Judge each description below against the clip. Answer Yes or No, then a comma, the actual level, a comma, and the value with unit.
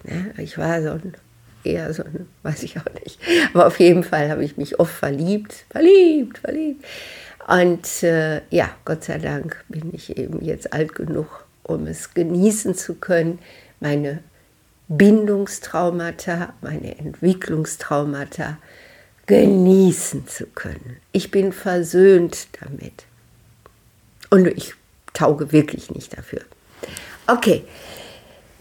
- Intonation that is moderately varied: Yes, average, 4.0 semitones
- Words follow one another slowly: Yes, slow, 120 wpm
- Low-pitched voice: No, medium, 175 Hz